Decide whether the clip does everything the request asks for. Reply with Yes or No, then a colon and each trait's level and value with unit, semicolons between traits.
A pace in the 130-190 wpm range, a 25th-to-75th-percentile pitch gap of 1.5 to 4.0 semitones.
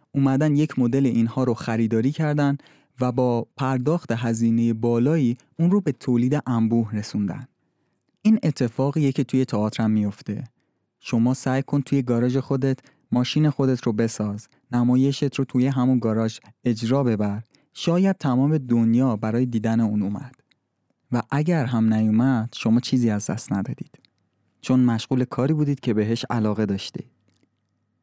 Yes: average, 140 wpm; average, 3.2 semitones